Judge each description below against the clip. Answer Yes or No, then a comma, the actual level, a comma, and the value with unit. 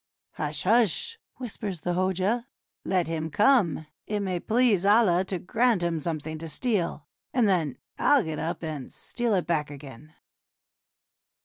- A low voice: No, medium, 180 Hz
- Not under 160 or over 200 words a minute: No, average, 150 wpm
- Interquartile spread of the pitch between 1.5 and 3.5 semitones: No, wide, 5.6 semitones